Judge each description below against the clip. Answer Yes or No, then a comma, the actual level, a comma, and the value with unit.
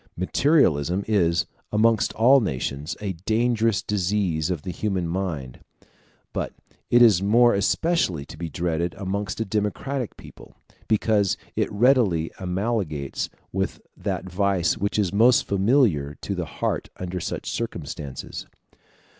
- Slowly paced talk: Yes, slow, 130 wpm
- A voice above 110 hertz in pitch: No, low, 100 Hz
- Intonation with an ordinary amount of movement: Yes, average, 4.7 semitones